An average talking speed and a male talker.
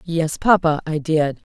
No: average, 160 wpm; female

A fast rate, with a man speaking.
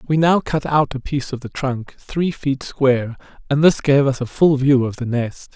Yes: fast, 240 wpm; male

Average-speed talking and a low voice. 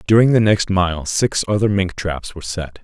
No: fast, 210 wpm; very low, 95 Hz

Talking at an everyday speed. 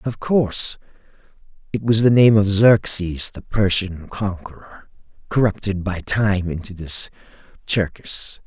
No: slow, 105 wpm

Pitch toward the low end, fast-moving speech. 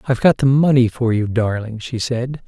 Yes: low, 120 Hz; fast, 220 wpm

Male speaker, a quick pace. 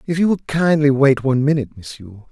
Yes: male; fast, 235 wpm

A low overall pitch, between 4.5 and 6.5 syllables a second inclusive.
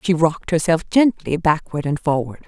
No: medium, 165 Hz; 5.1 syllables/s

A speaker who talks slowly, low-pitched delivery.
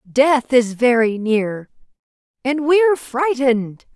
No: slow, 120 wpm; very high, 255 Hz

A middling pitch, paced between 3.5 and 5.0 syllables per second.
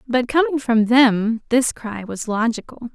No: high, 235 Hz; 4.0 syllables/s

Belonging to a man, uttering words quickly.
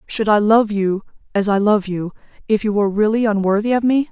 No: female; fast, 220 wpm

